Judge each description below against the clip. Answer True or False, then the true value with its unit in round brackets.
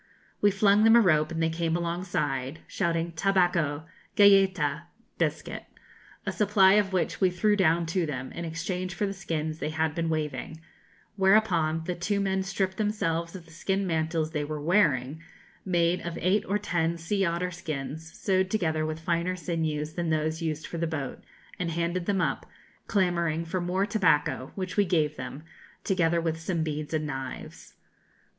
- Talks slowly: False (170 wpm)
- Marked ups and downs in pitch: False (3.0 semitones)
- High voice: False (170 Hz)